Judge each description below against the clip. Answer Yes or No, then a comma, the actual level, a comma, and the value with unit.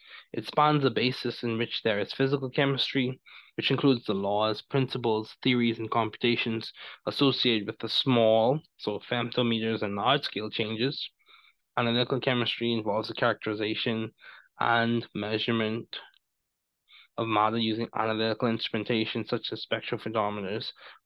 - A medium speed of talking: No, slow, 125 wpm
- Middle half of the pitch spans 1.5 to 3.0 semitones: Yes, narrow, 2.6 semitones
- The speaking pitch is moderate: No, low, 115 Hz